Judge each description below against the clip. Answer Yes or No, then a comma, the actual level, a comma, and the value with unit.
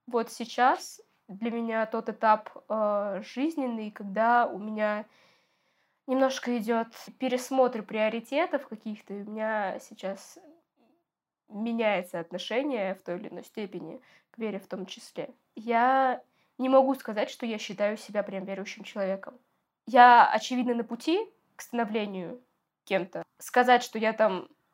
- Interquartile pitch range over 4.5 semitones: No, average, 3.3 semitones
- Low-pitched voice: No, high, 230 Hz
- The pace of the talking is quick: No, average, 130 wpm